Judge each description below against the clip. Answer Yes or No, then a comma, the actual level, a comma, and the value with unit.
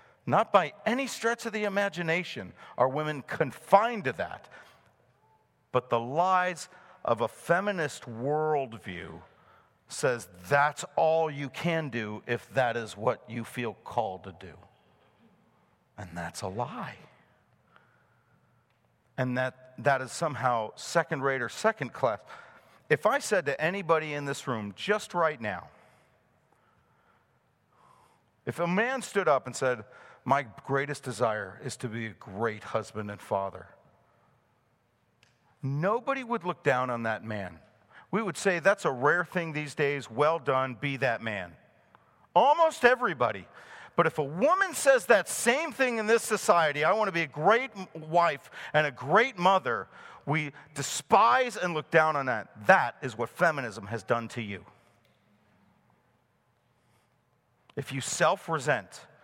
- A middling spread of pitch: No, wide, 7.4 semitones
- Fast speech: No, average, 140 wpm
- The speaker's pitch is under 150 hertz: Yes, medium, 140 Hz